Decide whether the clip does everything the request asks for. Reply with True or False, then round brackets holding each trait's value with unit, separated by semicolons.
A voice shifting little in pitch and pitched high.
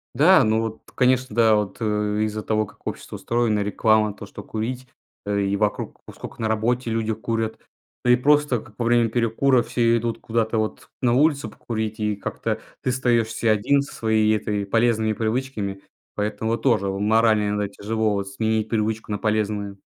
False (1.9 semitones; 110 Hz)